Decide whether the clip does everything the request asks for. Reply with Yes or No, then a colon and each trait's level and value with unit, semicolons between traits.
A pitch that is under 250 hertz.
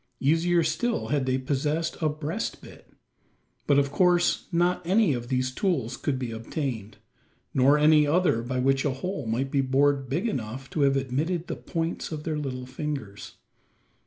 Yes: medium, 140 Hz